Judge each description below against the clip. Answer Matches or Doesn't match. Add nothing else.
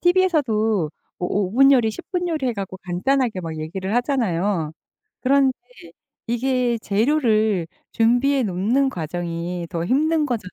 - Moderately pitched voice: Doesn't match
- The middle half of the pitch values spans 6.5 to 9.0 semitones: Matches